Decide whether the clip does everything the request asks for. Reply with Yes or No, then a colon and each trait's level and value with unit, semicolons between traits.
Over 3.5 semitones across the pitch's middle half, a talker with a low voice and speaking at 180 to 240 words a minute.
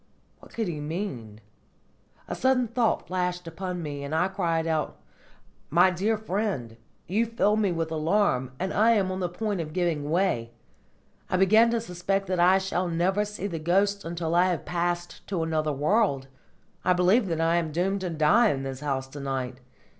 No: average, 3.9 semitones; medium, 175 Hz; average, 185 wpm